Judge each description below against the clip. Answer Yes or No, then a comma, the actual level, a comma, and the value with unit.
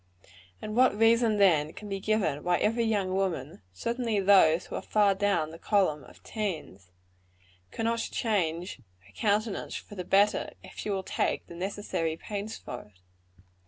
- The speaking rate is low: No, average, 165 wpm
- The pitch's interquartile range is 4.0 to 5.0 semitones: Yes, average, 4.5 semitones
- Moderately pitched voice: No, high, 195 Hz